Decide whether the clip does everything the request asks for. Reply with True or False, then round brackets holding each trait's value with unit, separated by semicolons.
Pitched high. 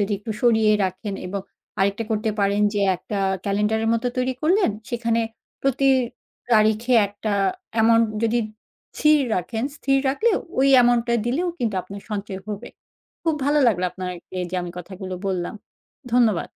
True (220 Hz)